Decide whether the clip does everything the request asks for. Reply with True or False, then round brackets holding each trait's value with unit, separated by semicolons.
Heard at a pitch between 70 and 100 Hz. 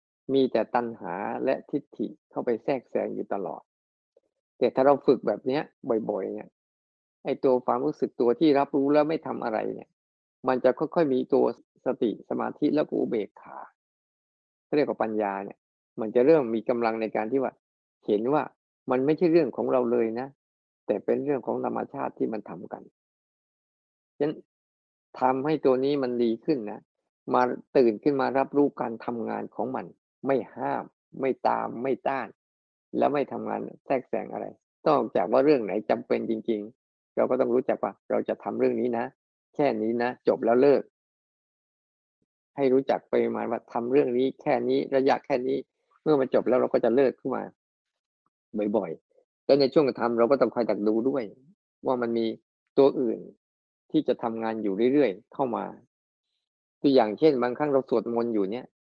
False (120 Hz)